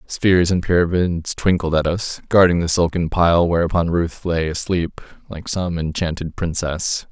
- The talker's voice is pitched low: Yes, very low, 85 Hz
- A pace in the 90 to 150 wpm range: Yes, average, 145 wpm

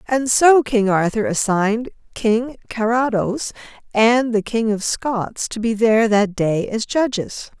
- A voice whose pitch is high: Yes, high, 225 Hz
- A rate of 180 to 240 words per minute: No, average, 150 wpm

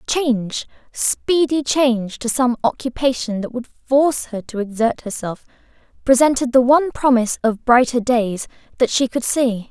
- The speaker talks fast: No, average, 150 wpm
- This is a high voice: Yes, high, 245 Hz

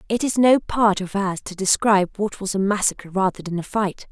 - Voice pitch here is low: No, high, 200 Hz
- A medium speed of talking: No, fast, 235 wpm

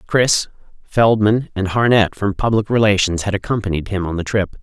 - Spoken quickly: No, average, 170 wpm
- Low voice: Yes, low, 100 Hz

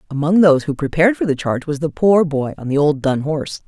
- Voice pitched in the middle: Yes, medium, 155 Hz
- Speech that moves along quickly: Yes, fast, 260 wpm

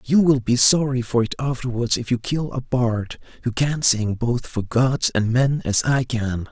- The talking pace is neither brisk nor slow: No, fast, 210 wpm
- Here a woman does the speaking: No, male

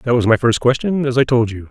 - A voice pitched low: Yes, low, 125 Hz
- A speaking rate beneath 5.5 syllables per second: No, 6.0 syllables/s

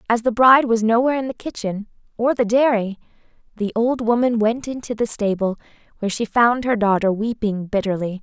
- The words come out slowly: No, average, 180 wpm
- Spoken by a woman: Yes, female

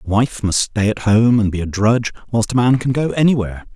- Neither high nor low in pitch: No, low, 110 Hz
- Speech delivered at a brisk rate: Yes, fast, 255 wpm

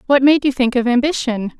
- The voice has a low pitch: No, very high, 255 Hz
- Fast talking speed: Yes, fast, 225 wpm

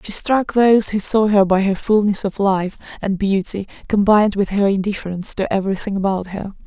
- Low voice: No, high, 200 Hz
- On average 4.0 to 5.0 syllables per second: No, 5.6 syllables/s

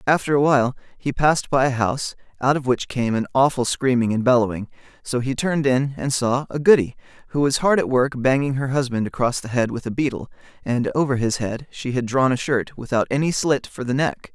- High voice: No, low, 130 Hz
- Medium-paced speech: No, fast, 225 wpm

